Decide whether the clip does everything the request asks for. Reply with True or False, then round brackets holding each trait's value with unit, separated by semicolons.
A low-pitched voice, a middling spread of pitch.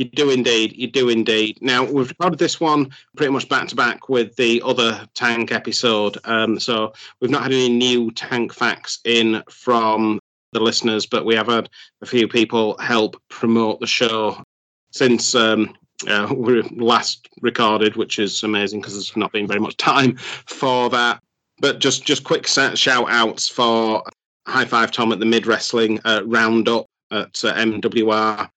False (115 Hz; 1.9 semitones)